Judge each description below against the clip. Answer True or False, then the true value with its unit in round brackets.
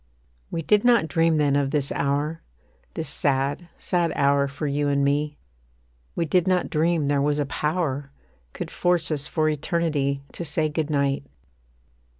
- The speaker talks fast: False (160 wpm)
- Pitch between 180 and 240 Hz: False (150 Hz)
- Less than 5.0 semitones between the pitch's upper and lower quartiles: True (2.7 semitones)